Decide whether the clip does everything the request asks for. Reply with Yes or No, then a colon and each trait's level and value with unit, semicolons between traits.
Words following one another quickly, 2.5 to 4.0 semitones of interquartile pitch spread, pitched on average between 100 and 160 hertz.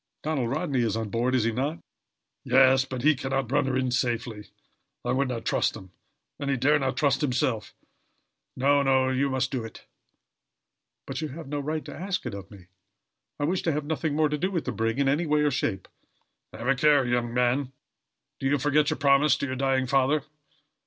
Yes: fast, 215 wpm; average, 2.9 semitones; low, 135 Hz